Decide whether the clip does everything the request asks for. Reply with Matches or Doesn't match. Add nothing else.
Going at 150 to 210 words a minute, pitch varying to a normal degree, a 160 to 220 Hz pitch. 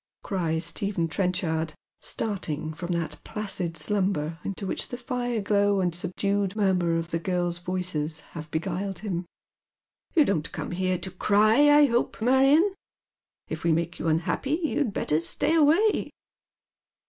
Matches